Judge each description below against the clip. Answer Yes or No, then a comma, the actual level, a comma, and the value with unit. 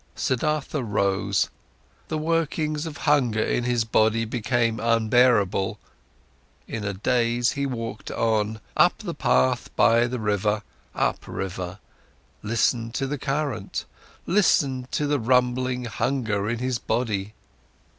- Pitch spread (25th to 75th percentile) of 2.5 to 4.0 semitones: Yes, average, 3.4 semitones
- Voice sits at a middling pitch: No, low, 120 Hz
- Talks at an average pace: No, slow, 120 wpm